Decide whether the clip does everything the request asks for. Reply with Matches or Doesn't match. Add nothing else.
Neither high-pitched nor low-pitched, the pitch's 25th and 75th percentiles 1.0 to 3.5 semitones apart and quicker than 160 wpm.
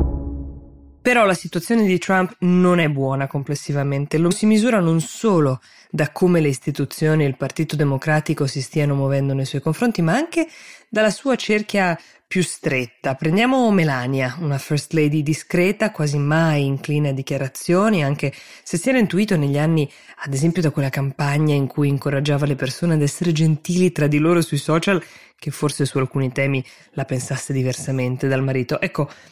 Doesn't match